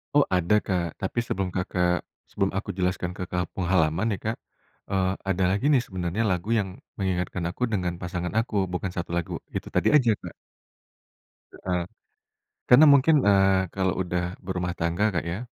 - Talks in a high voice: No, very low, 95 Hz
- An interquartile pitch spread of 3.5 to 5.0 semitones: No, narrow, 2.4 semitones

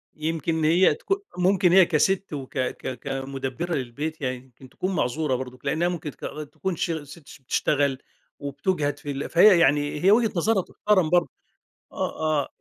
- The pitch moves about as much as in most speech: Yes, average, 4.3 semitones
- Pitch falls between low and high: Yes, medium, 155 Hz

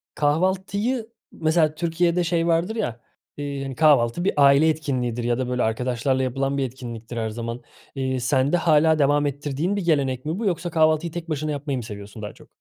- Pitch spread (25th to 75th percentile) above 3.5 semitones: Yes, average, 4.5 semitones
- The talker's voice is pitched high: No, medium, 145 Hz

